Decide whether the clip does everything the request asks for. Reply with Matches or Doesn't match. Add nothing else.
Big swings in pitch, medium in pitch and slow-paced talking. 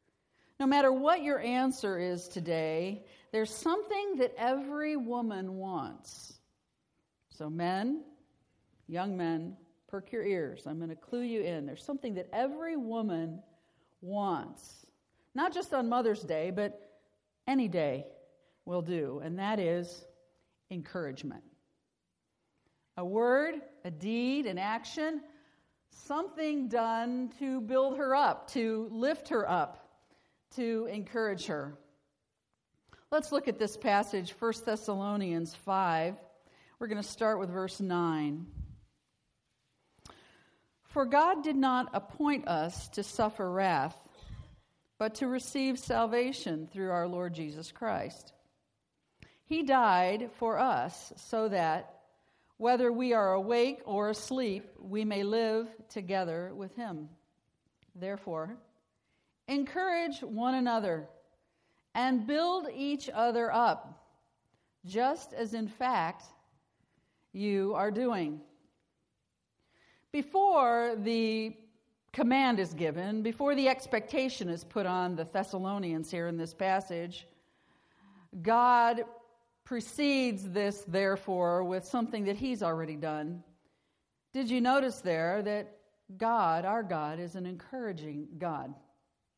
Doesn't match